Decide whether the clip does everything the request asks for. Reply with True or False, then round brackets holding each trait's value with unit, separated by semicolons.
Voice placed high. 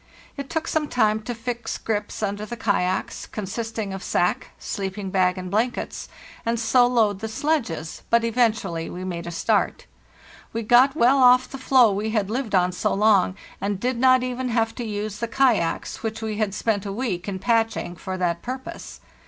True (220 Hz)